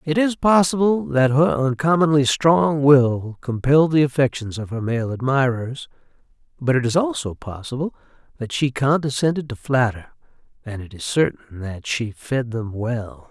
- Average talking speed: Yes, average, 155 wpm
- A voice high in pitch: No, low, 130 Hz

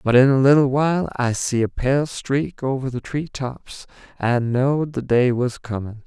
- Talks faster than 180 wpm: Yes, average, 190 wpm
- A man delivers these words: Yes, male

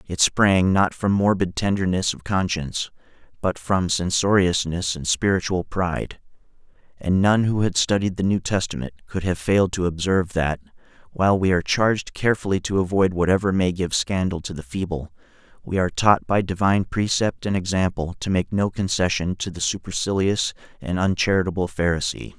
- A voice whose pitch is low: Yes, very low, 95 Hz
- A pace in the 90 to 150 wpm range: No, average, 160 wpm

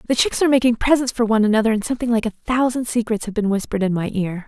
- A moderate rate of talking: No, fast, 270 wpm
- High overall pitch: Yes, high, 230 Hz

